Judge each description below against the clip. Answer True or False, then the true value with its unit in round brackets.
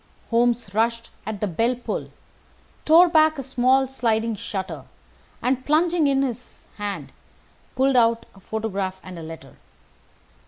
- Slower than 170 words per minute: True (135 wpm)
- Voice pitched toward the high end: True (235 Hz)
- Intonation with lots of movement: False (4.5 semitones)